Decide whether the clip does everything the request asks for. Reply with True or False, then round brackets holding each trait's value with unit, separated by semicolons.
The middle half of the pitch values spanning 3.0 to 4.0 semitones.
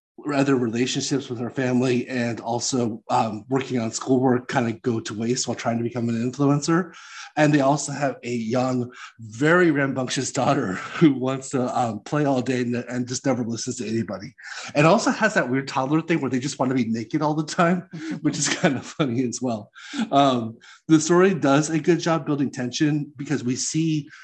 True (3.4 semitones)